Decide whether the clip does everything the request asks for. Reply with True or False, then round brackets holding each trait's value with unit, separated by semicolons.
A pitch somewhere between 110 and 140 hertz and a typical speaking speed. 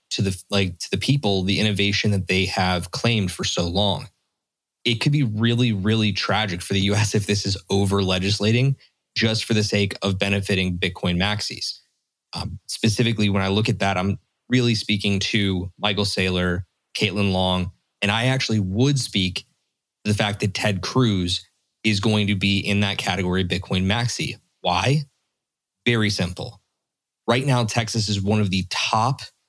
False (100 Hz; 170 wpm)